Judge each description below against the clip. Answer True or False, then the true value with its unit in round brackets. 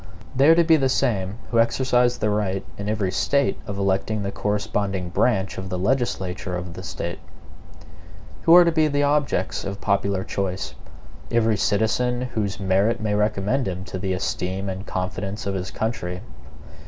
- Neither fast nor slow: True (170 wpm)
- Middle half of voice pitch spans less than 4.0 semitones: False (4.3 semitones)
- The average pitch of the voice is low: True (100 Hz)